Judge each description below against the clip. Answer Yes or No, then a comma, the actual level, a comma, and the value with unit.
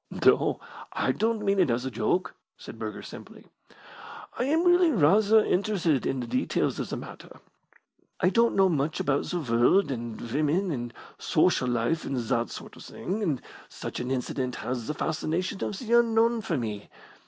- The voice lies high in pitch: No, medium, 160 Hz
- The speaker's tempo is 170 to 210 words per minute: Yes, average, 175 wpm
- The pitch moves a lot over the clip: Yes, wide, 8.8 semitones